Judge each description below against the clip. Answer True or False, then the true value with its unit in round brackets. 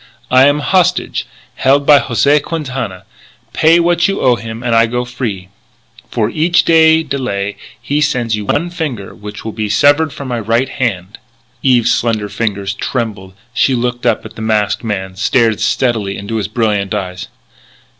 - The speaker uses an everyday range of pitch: True (5.0 semitones)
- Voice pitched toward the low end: True (120 Hz)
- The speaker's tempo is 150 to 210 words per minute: True (175 wpm)